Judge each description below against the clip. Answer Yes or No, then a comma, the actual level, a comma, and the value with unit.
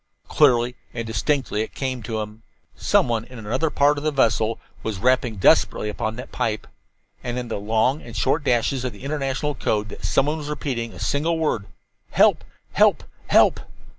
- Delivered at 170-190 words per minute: Yes, average, 180 wpm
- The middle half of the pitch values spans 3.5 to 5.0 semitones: Yes, average, 4.2 semitones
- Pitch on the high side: No, low, 125 Hz